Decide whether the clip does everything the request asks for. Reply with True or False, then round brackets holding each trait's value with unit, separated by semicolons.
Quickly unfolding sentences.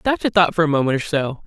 True (330 wpm)